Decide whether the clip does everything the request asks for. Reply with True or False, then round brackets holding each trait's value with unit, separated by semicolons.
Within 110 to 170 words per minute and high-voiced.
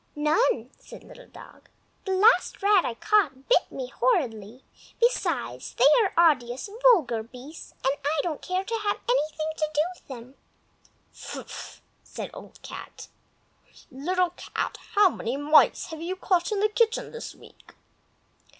True (150 wpm; 320 Hz)